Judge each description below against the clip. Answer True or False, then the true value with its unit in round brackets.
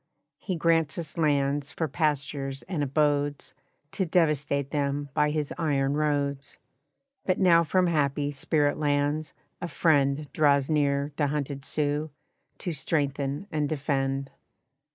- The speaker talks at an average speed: False (130 wpm)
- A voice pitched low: False (145 Hz)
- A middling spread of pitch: False (1.8 semitones)